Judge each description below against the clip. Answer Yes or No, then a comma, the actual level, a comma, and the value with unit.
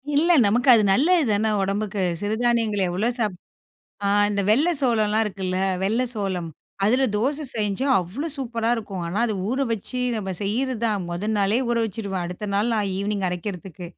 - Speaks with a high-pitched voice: Yes, high, 215 Hz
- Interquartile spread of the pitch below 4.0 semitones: Yes, average, 3.3 semitones